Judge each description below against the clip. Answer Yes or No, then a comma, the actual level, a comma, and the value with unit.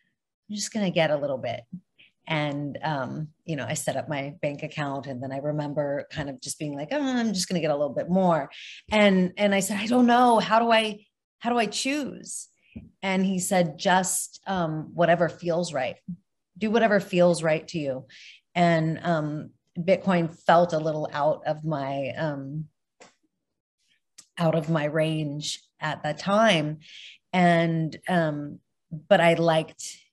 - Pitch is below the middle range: No, medium, 165 Hz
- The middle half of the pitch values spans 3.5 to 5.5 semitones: Yes, average, 4.0 semitones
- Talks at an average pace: Yes, average, 165 wpm